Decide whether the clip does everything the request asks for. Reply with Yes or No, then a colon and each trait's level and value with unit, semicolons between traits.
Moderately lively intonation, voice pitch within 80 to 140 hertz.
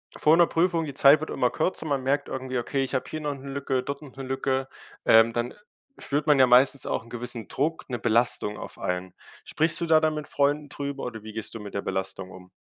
Yes: average, 3.8 semitones; low, 135 Hz